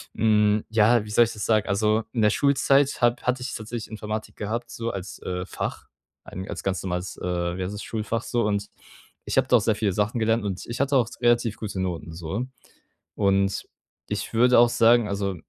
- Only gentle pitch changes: No, average, 3.1 semitones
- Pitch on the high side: No, low, 110 Hz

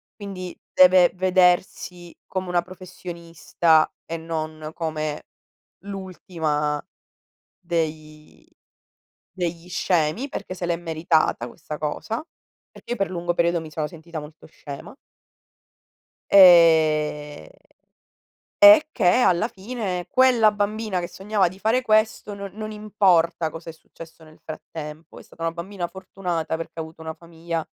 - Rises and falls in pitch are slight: No, average, 3.0 semitones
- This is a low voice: No, medium, 170 Hz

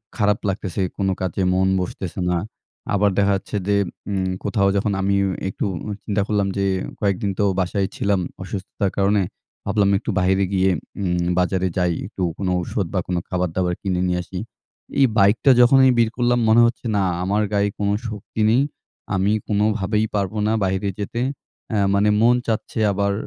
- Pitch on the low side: Yes, low, 100 Hz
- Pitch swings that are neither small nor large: No, narrow, 1.9 semitones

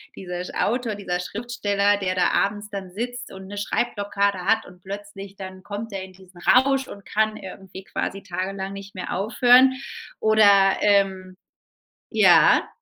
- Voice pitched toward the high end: Yes, high, 200 Hz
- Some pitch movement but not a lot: No, narrow, 2.1 semitones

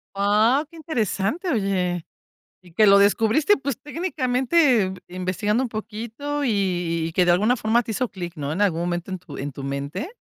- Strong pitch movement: Yes, wide, 6.0 semitones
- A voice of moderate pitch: No, high, 205 Hz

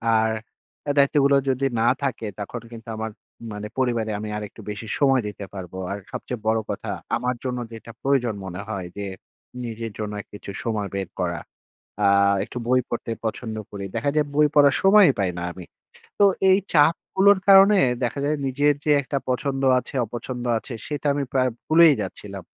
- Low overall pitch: Yes, low, 120 Hz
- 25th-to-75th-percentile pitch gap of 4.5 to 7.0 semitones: Yes, average, 4.9 semitones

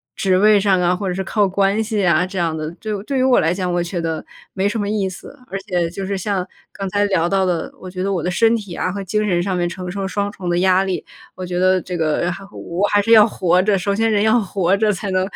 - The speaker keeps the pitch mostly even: Yes, narrow, 2.2 semitones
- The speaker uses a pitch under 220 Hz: Yes, high, 190 Hz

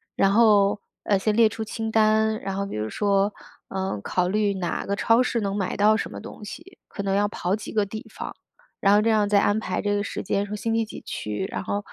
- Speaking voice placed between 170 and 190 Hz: No, high, 205 Hz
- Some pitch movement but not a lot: No, narrow, 1.7 semitones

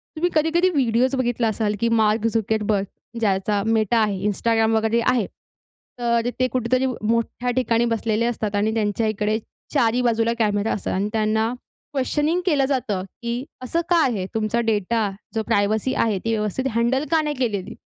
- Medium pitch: No, high, 225 Hz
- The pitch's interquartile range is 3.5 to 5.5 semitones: No, average, 2.7 semitones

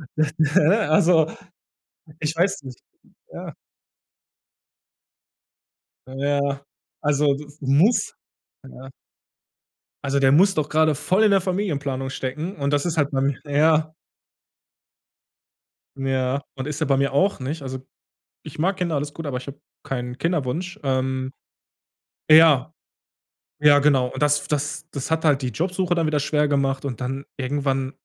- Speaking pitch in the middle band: Yes, medium, 145 Hz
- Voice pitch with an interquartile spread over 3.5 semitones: No, average, 2.9 semitones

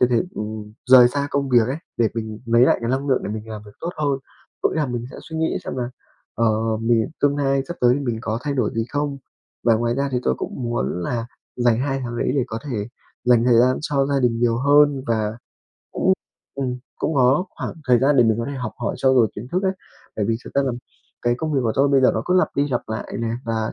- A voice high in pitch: No, low, 125 Hz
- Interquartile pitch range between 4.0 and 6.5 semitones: No, average, 3.3 semitones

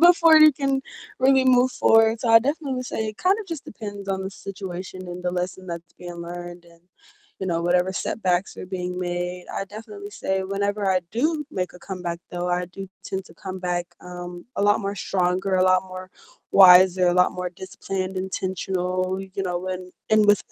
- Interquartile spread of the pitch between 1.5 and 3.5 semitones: Yes, narrow, 2.5 semitones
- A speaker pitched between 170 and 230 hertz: Yes, medium, 185 Hz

